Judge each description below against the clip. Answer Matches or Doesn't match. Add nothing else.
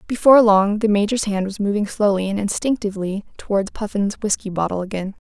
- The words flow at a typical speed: Matches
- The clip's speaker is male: Doesn't match